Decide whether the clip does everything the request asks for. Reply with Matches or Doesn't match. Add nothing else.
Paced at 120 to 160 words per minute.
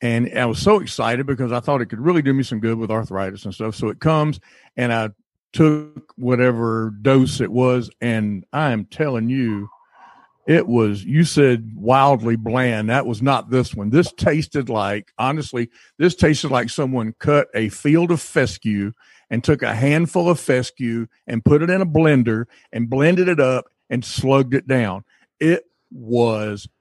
Doesn't match